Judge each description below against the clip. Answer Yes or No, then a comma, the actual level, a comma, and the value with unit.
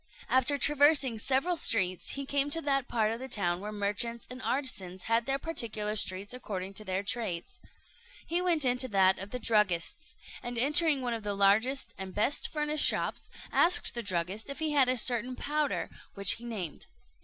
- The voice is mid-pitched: No, high, 235 Hz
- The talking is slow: No, average, 190 wpm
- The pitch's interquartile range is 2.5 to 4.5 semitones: No, wide, 5.5 semitones